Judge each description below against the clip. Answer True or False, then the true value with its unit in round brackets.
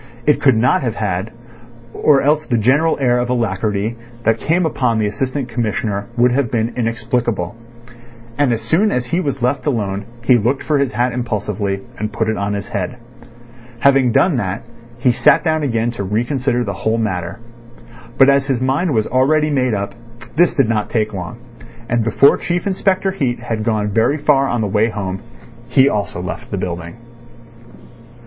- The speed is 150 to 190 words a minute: True (180 wpm)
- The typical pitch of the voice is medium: False (120 Hz)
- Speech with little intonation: False (4.3 semitones)